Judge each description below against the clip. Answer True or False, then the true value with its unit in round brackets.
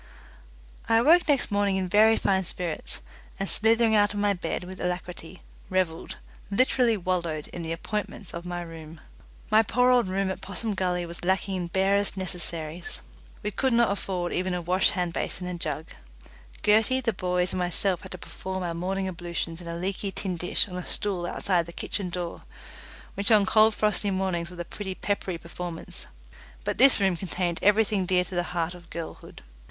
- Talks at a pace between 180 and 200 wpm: True (185 wpm)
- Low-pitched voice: False (185 Hz)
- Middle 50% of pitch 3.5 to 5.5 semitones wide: False (2.6 semitones)